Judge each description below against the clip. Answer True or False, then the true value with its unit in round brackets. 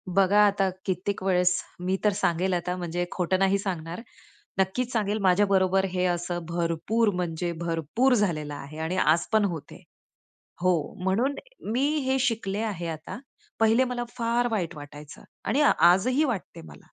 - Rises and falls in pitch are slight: False (3.8 semitones)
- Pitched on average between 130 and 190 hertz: True (185 Hz)